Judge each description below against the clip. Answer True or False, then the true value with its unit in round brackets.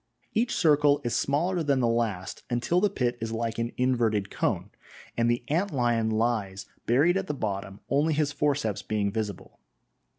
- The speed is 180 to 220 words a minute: False (170 wpm)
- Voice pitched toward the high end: False (120 Hz)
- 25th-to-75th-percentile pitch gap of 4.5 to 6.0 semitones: True (4.9 semitones)